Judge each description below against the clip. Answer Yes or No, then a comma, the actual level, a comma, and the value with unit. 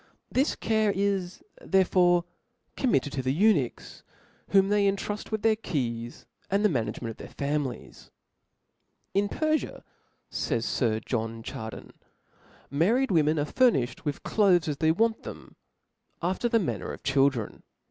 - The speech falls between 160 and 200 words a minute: No, average, 150 wpm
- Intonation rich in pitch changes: Yes, wide, 7.5 semitones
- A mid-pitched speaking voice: Yes, medium, 175 Hz